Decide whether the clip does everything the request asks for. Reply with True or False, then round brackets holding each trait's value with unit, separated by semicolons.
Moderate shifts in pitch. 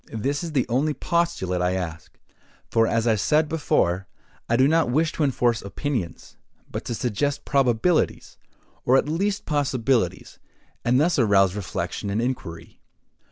False (6.4 semitones)